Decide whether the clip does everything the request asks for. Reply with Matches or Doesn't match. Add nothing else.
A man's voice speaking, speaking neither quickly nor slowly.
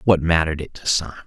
Doesn't match